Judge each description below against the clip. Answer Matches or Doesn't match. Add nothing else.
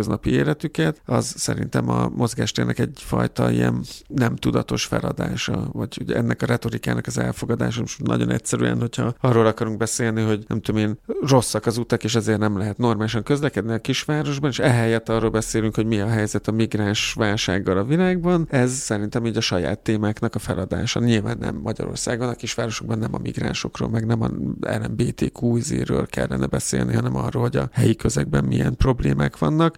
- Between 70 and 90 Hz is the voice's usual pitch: Doesn't match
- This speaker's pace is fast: Matches